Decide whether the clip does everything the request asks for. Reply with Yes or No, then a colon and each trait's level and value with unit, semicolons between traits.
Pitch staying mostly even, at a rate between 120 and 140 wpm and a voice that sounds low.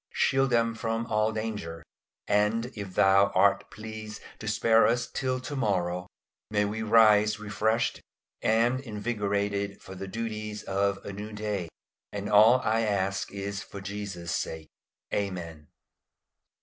Yes: narrow, 2.1 semitones; slow, 135 wpm; low, 105 Hz